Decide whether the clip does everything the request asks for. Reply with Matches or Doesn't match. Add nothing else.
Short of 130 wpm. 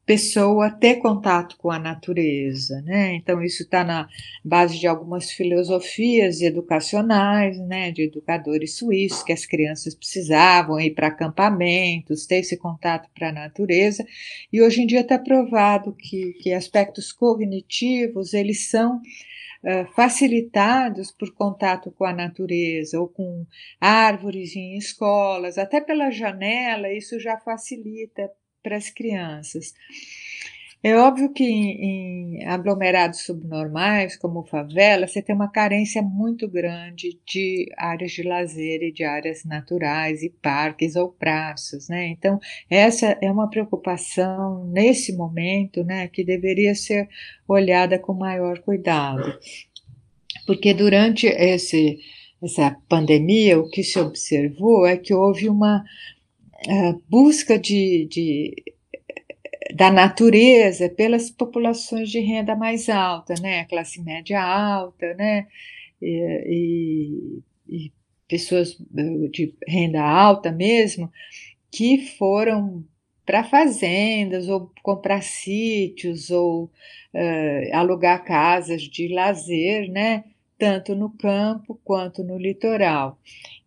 Matches